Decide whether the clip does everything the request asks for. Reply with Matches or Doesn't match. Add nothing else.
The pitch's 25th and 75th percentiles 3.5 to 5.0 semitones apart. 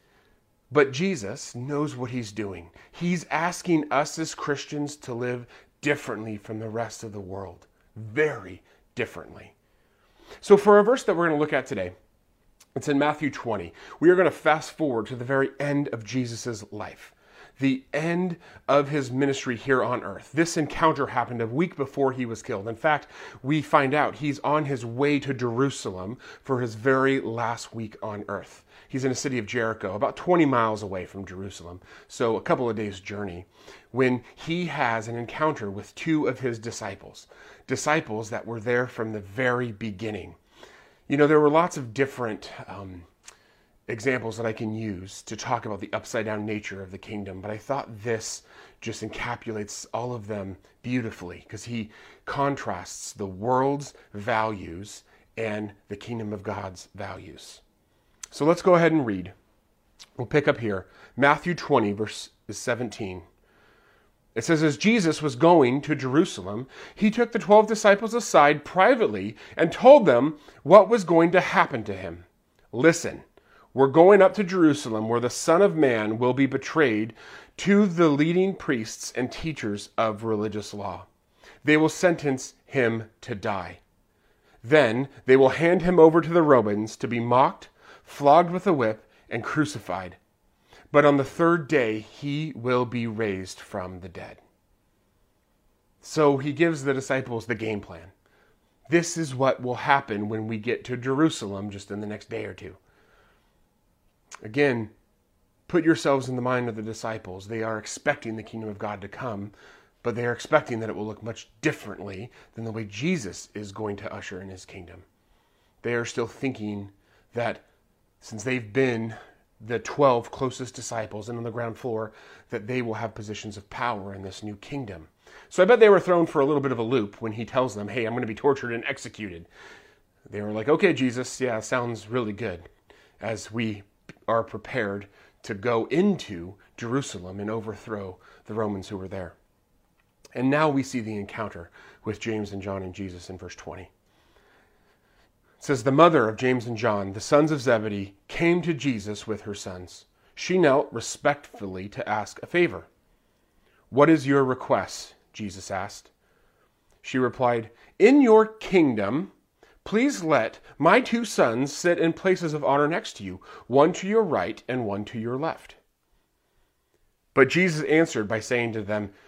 Doesn't match